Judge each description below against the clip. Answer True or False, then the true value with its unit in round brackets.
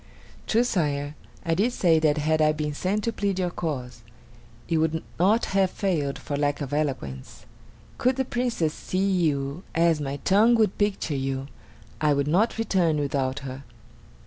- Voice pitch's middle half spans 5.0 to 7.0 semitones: True (5.3 semitones)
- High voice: False (160 Hz)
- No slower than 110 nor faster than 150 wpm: False (170 wpm)